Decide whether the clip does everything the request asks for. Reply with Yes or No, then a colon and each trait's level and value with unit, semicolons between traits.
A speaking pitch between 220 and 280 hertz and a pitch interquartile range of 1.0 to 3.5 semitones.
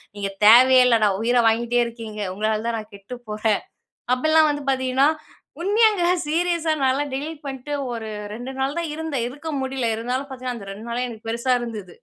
No: very high, 250 Hz; average, 4.3 semitones